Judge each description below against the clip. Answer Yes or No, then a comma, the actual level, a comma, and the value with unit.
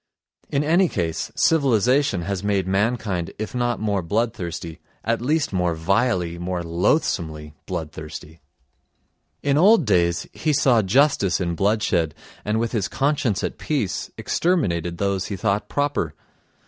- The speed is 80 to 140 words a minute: Yes, slow, 135 wpm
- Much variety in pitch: Yes, wide, 6.5 semitones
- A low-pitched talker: Yes, low, 100 Hz